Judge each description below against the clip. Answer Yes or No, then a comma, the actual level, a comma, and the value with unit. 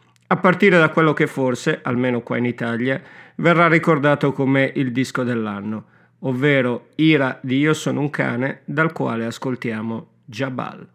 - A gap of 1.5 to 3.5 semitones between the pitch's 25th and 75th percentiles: No, average, 4.2 semitones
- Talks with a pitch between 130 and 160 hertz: Yes, low, 135 Hz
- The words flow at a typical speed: Yes, average, 150 wpm